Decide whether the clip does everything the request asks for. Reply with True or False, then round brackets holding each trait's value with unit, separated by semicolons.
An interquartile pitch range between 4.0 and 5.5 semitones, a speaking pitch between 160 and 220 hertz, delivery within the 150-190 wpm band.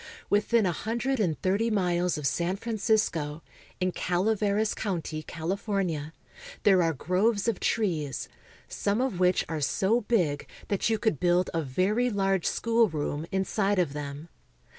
False (4.7 semitones; 190 Hz; 140 wpm)